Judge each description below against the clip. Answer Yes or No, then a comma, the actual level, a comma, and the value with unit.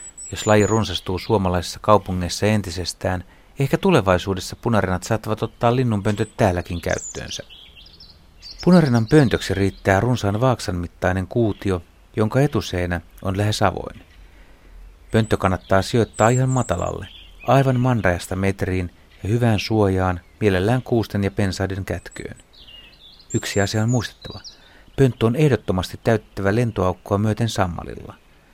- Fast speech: No, average, 110 wpm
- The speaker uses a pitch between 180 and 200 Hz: No, low, 100 Hz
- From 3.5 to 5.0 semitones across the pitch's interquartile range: Yes, average, 3.8 semitones